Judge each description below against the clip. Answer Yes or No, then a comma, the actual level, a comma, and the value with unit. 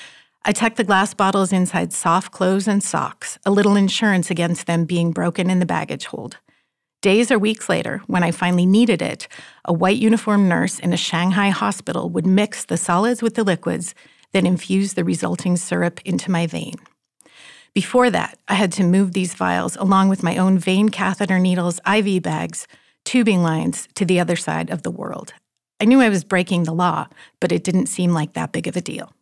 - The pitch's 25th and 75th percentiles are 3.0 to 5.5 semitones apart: No, narrow, 2.4 semitones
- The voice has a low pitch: No, high, 190 Hz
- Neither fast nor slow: Yes, average, 195 wpm